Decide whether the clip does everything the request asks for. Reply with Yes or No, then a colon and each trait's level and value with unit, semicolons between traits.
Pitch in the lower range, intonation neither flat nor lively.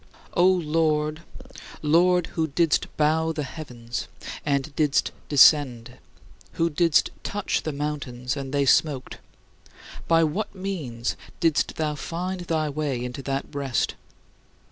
No: medium, 150 Hz; average, 3.1 semitones